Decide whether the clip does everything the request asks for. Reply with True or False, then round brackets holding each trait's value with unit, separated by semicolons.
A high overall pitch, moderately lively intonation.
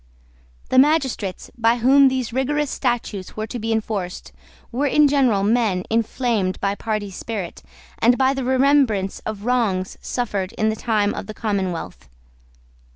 True (225 Hz; 4.3 semitones)